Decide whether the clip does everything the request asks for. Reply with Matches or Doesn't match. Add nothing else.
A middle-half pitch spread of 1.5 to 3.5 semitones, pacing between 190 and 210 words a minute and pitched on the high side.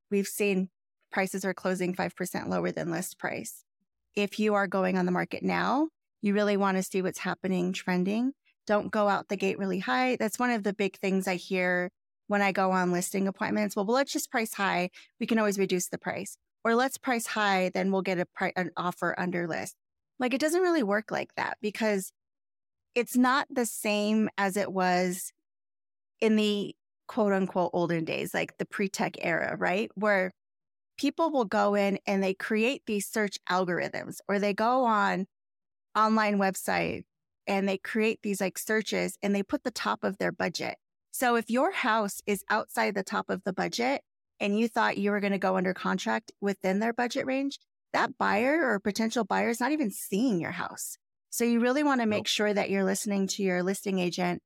Matches